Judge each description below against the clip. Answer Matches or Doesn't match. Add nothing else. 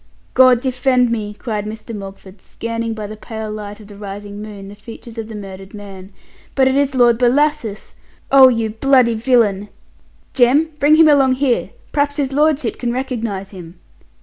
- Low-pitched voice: Doesn't match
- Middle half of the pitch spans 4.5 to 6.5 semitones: Doesn't match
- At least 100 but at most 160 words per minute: Doesn't match